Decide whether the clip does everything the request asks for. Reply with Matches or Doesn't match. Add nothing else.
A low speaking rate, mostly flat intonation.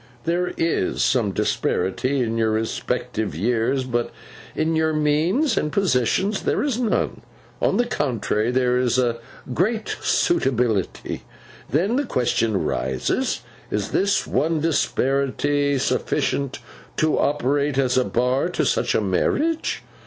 Doesn't match